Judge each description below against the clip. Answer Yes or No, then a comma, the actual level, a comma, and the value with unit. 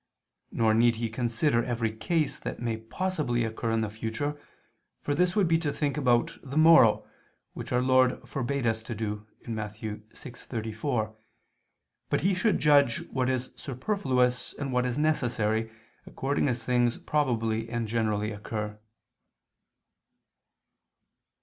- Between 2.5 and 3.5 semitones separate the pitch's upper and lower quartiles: No, average, 4.0 semitones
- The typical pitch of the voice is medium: No, low, 120 Hz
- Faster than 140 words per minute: No, slow, 135 wpm